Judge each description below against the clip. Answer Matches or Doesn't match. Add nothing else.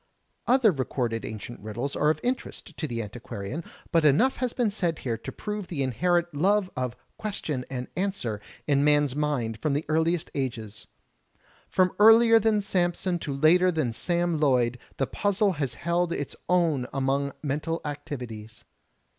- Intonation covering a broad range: Matches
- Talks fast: Doesn't match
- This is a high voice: Doesn't match